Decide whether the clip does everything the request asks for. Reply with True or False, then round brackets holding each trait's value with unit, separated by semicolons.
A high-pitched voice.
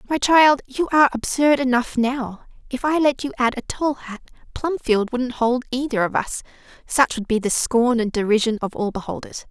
True (250 Hz)